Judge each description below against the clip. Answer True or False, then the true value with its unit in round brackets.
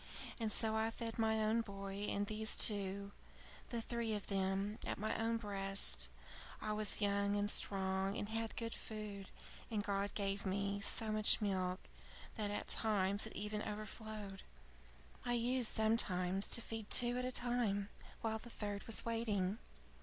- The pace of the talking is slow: False (160 wpm)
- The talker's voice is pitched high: True (210 Hz)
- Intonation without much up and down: True (2.0 semitones)